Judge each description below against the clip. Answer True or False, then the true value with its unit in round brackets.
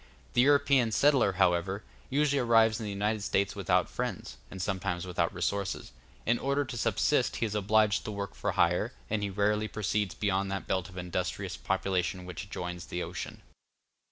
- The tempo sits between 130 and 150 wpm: False (175 wpm)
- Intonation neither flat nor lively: True (3.2 semitones)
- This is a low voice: True (100 Hz)